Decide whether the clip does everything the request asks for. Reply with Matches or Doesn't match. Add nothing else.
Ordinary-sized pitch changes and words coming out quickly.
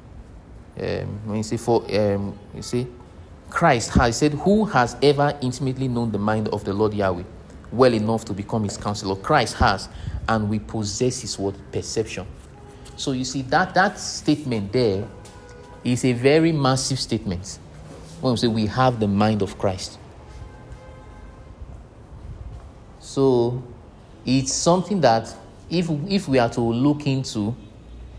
Doesn't match